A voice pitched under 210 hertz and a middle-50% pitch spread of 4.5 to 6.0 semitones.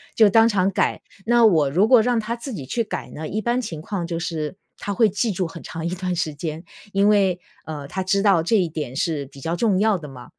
Yes: medium, 185 Hz; average, 5.0 semitones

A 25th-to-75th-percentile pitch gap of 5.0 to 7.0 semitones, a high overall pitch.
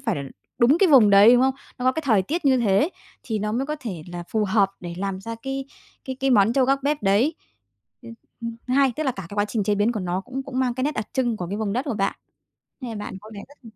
No: average, 4.6 semitones; high, 230 Hz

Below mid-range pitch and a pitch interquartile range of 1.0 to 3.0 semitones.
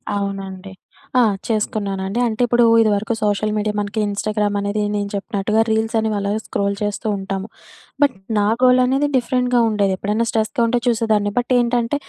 No: high, 215 Hz; narrow, 2.5 semitones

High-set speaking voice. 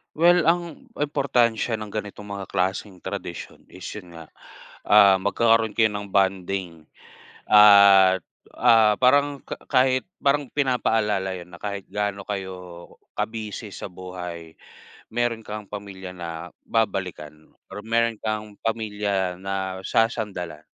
No: low, 105 Hz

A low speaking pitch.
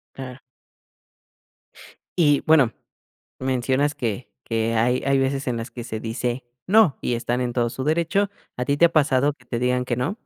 Yes: low, 130 Hz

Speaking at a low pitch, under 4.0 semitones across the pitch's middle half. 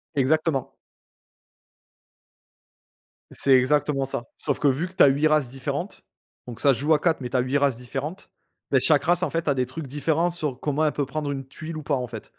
No: medium, 145 Hz; average, 2.8 semitones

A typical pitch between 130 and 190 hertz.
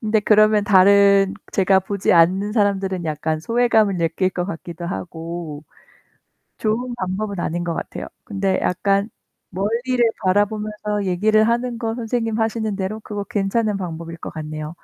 No: high, 200 Hz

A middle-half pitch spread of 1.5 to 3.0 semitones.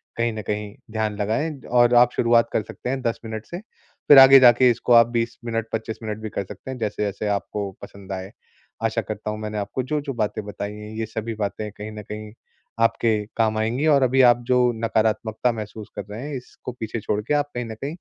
Yes: narrow, 2.4 semitones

